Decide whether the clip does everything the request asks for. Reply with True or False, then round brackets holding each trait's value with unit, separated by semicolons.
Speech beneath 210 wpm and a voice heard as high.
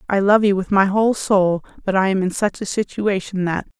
False (235 wpm; 195 Hz)